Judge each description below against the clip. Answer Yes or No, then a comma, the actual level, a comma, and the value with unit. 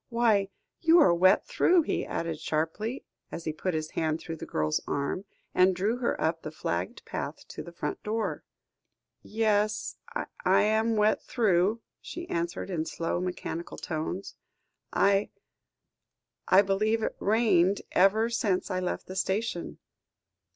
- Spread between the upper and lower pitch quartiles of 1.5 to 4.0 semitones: No, average, 4.4 semitones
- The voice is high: Yes, high, 195 Hz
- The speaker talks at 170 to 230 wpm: No, average, 145 wpm